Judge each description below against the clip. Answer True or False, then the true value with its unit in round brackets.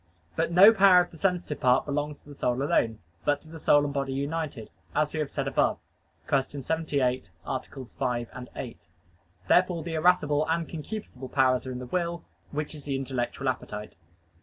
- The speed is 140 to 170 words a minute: False (185 wpm)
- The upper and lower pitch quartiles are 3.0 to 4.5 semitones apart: True (3.7 semitones)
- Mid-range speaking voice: True (145 Hz)